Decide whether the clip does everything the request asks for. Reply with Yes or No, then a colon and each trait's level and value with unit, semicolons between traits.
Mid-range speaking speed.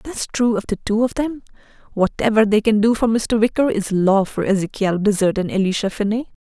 Yes: average, 195 wpm